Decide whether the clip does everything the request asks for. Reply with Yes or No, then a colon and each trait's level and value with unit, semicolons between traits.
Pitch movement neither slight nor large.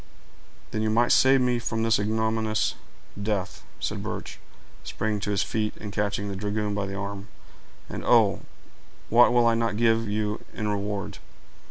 No: narrow, 1.8 semitones